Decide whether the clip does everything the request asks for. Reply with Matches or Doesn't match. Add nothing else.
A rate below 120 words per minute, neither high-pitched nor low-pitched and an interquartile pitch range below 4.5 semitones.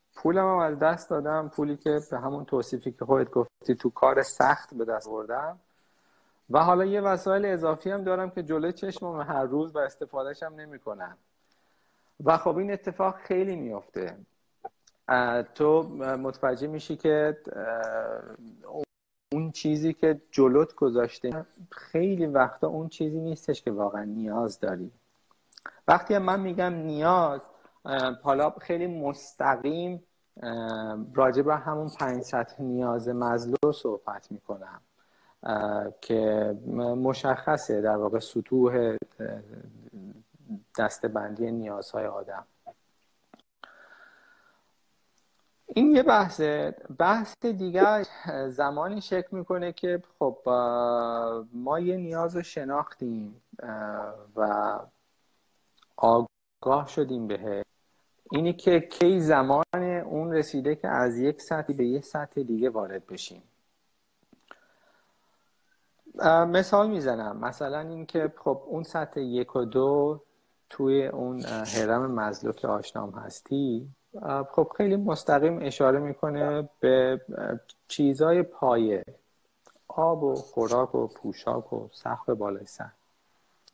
Doesn't match